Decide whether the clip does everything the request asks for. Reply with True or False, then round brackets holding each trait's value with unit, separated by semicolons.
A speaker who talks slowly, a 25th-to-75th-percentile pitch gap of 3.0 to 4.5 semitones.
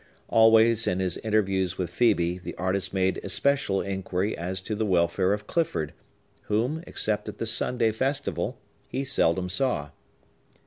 False (145 wpm; 3.6 semitones)